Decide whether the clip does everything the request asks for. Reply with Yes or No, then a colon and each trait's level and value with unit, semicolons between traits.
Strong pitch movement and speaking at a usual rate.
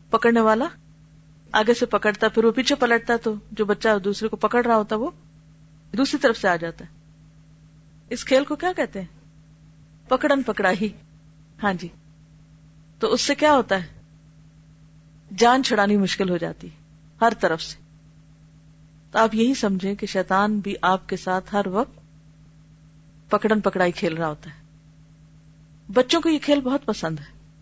Yes: wide, 6.1 semitones; average, 160 wpm